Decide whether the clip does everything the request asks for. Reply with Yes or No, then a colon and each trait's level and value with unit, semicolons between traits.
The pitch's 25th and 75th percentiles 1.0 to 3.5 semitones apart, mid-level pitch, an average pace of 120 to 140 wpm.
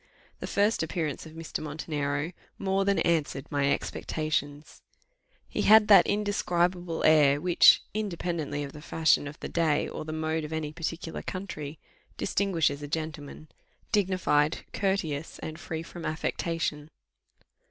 Yes: average, 3.1 semitones; medium, 160 Hz; slow, 135 wpm